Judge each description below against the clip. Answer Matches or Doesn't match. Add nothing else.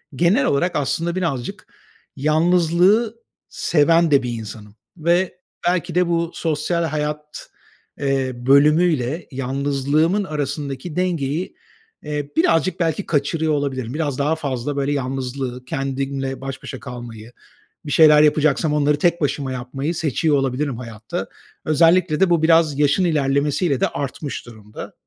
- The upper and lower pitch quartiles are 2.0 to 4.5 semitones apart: Matches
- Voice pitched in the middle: Matches